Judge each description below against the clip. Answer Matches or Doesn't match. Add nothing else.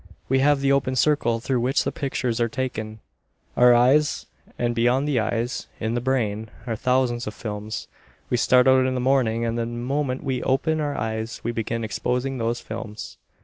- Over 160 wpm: Matches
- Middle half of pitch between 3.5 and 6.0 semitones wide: Doesn't match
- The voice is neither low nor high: Doesn't match